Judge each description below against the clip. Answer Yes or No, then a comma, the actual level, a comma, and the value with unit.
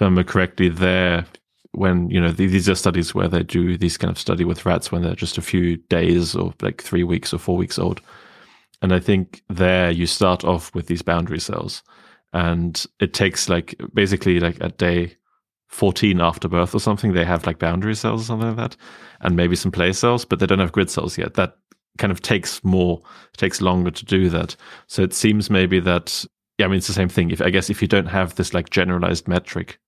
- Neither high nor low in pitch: No, very low, 90 Hz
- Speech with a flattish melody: Yes, narrow, 2.0 semitones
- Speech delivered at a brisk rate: Yes, fast, 220 wpm